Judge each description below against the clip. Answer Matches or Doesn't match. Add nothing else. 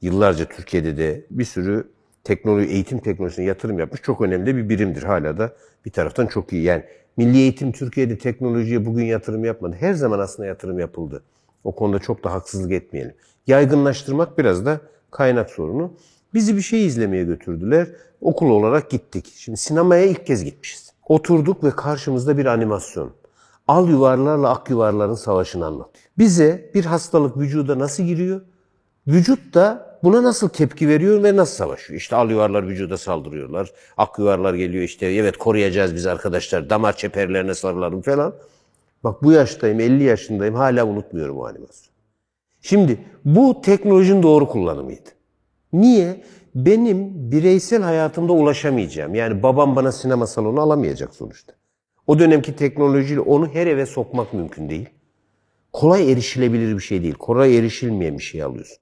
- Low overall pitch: Matches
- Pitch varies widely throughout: Matches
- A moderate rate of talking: Doesn't match